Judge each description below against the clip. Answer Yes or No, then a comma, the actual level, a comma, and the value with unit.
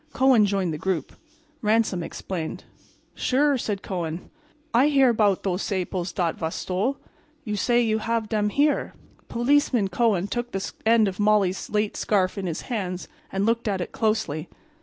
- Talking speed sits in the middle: Yes, average, 160 wpm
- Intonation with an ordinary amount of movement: Yes, average, 3.9 semitones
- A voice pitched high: Yes, high, 210 Hz